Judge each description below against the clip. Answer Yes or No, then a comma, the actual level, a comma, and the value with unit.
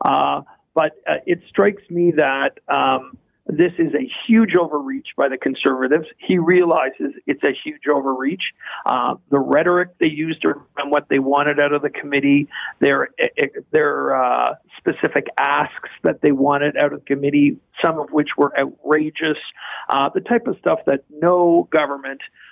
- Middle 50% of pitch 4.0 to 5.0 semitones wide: Yes, average, 4.7 semitones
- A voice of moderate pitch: Yes, medium, 155 Hz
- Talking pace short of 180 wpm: Yes, average, 160 wpm